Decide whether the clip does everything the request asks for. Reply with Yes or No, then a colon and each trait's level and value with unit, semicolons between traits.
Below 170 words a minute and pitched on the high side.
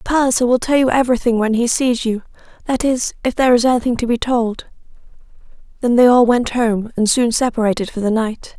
No: average, 195 wpm; high, 240 Hz